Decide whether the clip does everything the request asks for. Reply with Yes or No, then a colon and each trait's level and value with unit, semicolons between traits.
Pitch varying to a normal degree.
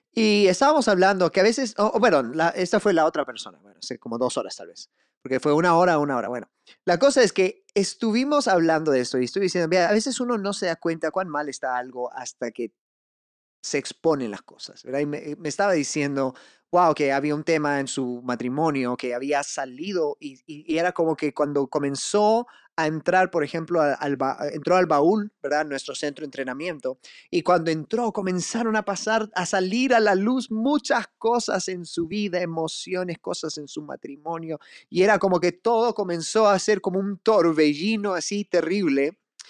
No: wide, 5.7 semitones